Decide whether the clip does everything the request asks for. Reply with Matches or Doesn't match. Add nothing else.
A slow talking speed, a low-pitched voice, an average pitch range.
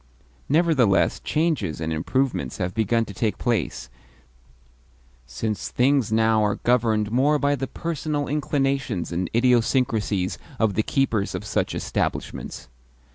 Matches